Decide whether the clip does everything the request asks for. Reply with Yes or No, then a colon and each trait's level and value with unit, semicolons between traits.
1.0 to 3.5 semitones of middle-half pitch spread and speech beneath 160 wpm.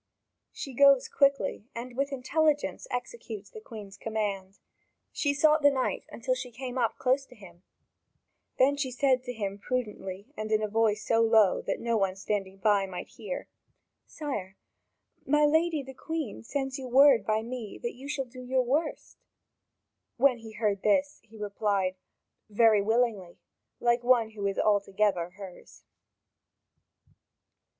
No: average, 4.6 semitones; average, 150 wpm